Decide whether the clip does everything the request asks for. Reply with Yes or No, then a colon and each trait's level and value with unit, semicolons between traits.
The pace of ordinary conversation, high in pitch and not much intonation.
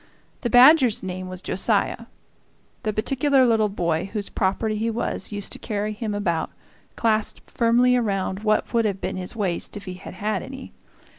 No: average, 170 wpm; high, 215 Hz; average, 3.3 semitones